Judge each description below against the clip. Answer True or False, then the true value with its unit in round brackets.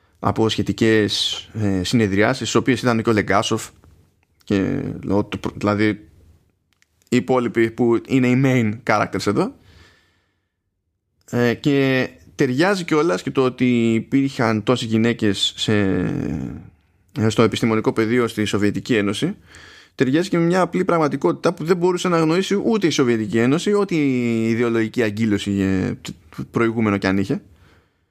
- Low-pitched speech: True (110 Hz)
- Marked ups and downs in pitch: False (4.7 semitones)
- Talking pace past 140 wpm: False (130 wpm)